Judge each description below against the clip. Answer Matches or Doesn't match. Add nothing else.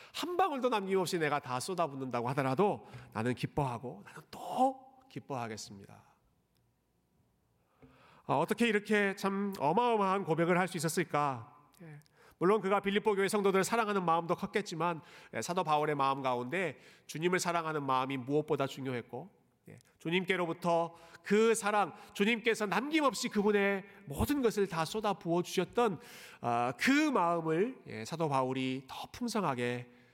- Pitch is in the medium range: Matches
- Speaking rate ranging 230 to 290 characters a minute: Doesn't match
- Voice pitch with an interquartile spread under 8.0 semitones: Matches